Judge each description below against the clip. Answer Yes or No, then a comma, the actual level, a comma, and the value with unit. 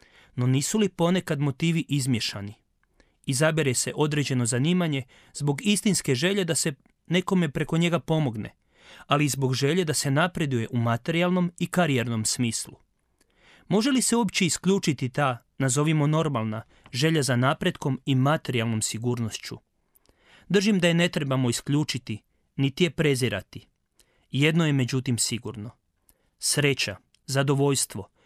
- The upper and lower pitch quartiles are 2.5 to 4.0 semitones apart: No, average, 5.1 semitones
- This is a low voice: No, medium, 145 Hz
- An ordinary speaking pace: Yes, average, 125 wpm